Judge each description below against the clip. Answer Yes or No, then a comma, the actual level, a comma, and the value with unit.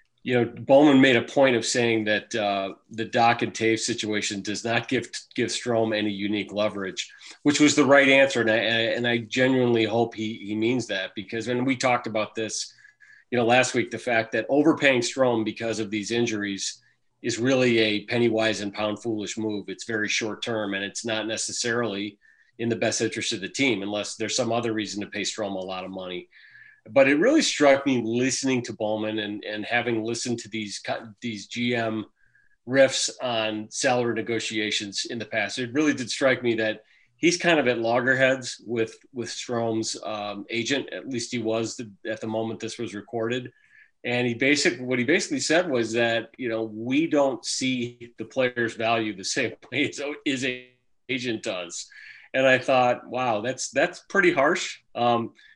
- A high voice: No, low, 115 Hz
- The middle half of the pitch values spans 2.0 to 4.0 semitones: Yes, narrow, 2.5 semitones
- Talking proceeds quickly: No, average, 190 wpm